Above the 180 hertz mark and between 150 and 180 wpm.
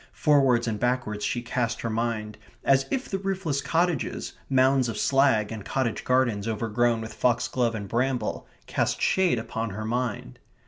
No: low, 120 Hz; average, 155 wpm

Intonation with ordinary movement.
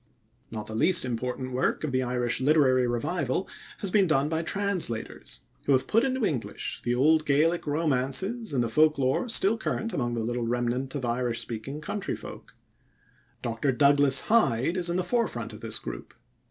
No: wide, 5.8 semitones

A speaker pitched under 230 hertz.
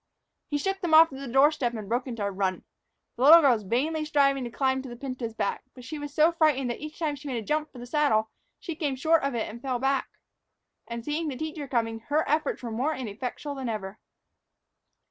No: very high, 270 Hz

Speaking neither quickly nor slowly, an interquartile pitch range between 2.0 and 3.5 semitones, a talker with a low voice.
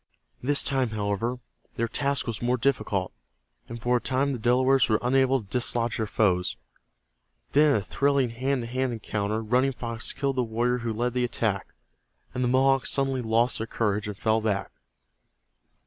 Yes: average, 180 wpm; average, 2.9 semitones; low, 120 Hz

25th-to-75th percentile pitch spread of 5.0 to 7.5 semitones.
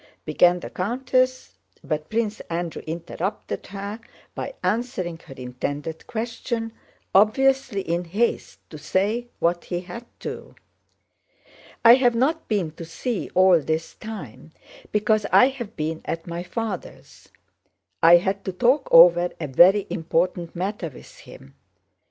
Yes: average, 5.3 semitones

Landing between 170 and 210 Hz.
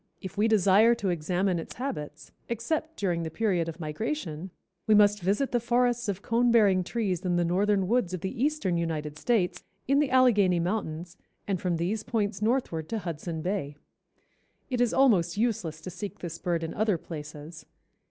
Yes: high, 190 Hz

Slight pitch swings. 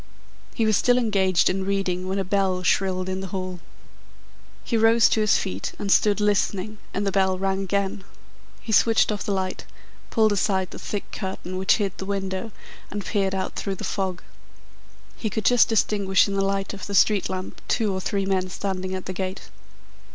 Yes: narrow, 1.6 semitones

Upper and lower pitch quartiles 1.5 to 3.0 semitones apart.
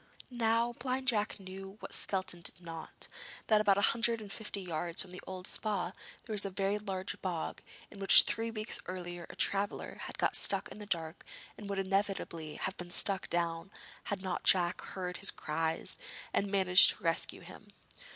Yes: average, 2.7 semitones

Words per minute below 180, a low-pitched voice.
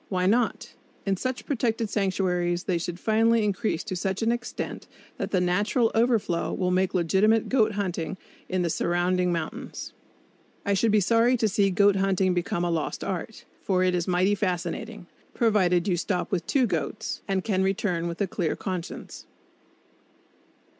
No: average, 165 wpm; high, 190 Hz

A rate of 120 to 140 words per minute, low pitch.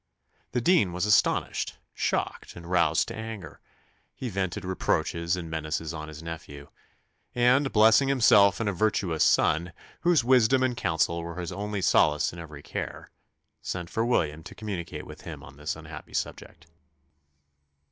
No: average, 155 wpm; very low, 90 Hz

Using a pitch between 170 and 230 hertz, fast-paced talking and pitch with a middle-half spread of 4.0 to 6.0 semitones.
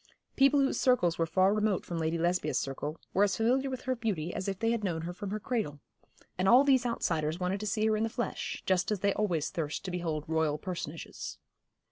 Yes: high, 190 Hz; fast, 225 wpm; average, 5.2 semitones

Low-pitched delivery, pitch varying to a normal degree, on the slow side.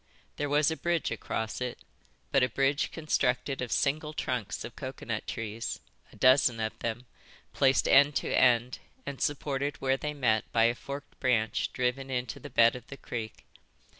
No: low, 130 Hz; average, 3.2 semitones; average, 170 wpm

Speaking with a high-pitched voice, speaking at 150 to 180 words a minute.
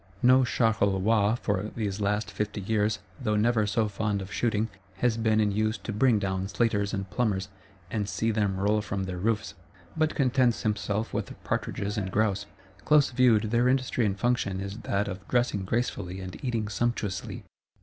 No: low, 105 Hz; average, 170 wpm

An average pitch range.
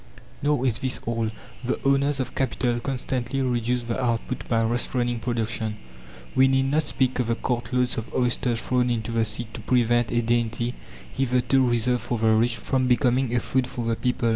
No: narrow, 1.7 semitones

